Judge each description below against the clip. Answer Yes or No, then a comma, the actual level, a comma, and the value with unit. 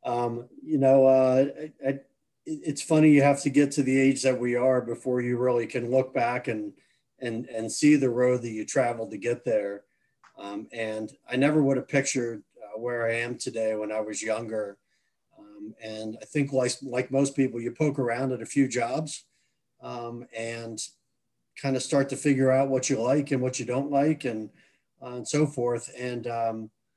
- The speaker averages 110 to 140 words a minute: No, average, 200 wpm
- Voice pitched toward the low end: Yes, low, 125 Hz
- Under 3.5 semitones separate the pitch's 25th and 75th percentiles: Yes, average, 2.8 semitones